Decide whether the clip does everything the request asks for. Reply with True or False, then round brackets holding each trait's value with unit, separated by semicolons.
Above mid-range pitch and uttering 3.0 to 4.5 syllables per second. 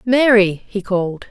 True (205 Hz; 4.2 syllables/s)